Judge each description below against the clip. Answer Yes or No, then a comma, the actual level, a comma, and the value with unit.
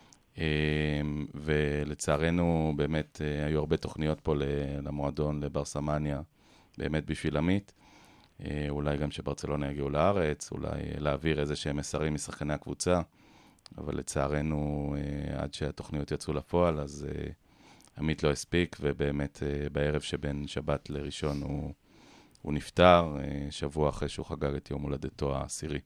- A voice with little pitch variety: Yes, narrow, 1.2 semitones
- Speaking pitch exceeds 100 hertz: No, very low, 75 Hz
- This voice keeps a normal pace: Yes, average, 115 wpm